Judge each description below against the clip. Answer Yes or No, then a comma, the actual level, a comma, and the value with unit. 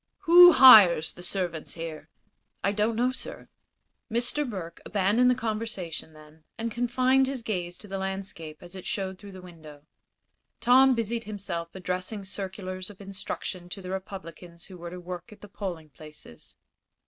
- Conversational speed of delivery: Yes, average, 160 wpm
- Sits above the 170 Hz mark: Yes, high, 190 Hz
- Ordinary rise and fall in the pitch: Yes, average, 4.4 semitones